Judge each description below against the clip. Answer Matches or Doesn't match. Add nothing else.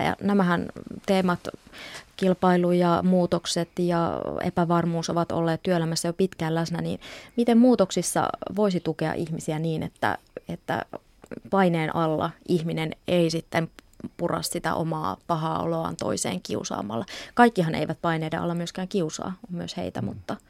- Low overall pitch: Doesn't match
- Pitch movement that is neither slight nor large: Doesn't match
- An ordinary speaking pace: Matches